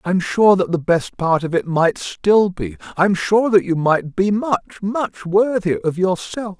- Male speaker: Yes, male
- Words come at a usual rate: No, fast, 220 wpm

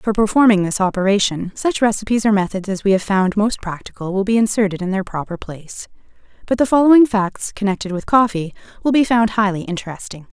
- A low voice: No, high, 205 Hz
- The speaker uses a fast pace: No, average, 190 wpm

